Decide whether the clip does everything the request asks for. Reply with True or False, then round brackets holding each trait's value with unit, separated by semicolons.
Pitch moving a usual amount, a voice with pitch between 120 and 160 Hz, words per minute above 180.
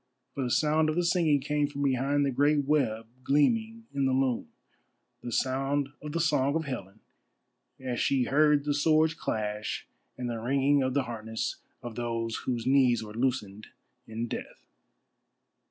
False (3.7 semitones; 135 Hz; 165 wpm)